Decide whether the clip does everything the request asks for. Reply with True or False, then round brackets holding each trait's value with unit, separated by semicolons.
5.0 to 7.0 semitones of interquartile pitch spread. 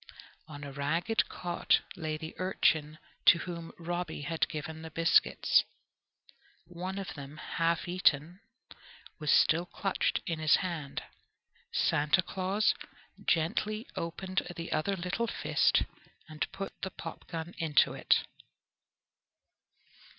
False (2.9 semitones)